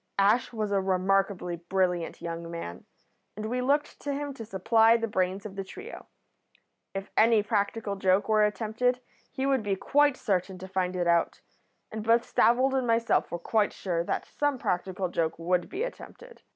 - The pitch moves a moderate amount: Yes, average, 4.2 semitones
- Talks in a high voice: Yes, high, 205 Hz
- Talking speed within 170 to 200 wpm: Yes, average, 180 wpm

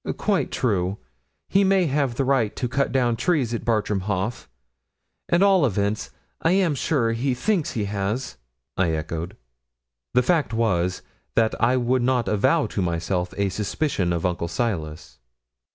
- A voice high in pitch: No, low, 115 Hz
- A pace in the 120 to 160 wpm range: Yes, average, 155 wpm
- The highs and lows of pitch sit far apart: Yes, wide, 6.2 semitones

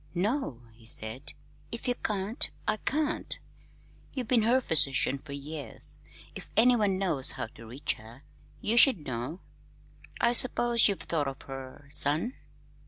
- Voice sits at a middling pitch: Yes, medium, 170 Hz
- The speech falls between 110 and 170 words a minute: Yes, average, 145 wpm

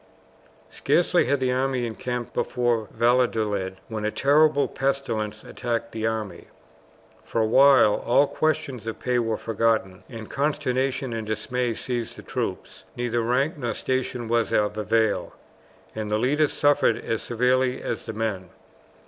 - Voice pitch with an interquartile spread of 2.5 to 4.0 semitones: Yes, average, 2.8 semitones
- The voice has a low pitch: Yes, low, 120 Hz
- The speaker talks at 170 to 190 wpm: No, average, 145 wpm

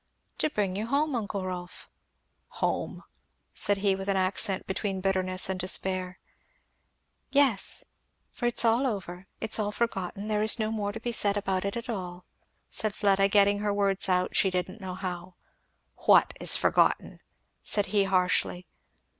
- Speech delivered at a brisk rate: No, average, 160 wpm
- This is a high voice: Yes, high, 195 Hz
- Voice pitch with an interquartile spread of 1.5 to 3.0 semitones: Yes, narrow, 2.4 semitones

